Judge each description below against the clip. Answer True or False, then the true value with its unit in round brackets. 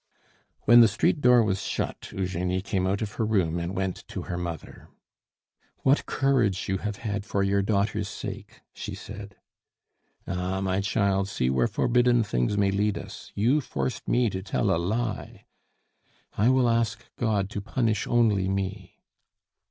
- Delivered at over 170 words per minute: False (160 wpm)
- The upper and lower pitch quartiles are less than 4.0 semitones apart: True (3.1 semitones)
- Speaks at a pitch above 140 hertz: False (100 Hz)